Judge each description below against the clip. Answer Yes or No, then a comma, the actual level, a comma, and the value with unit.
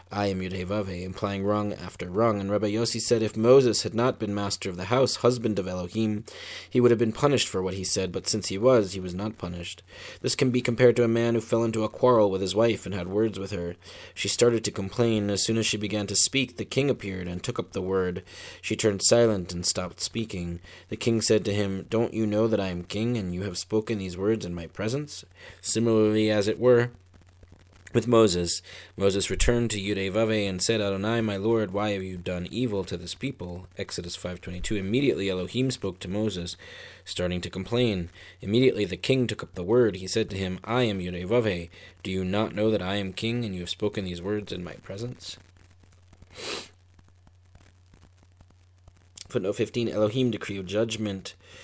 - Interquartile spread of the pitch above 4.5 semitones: No, average, 3.6 semitones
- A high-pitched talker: No, low, 100 Hz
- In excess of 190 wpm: Yes, fast, 205 wpm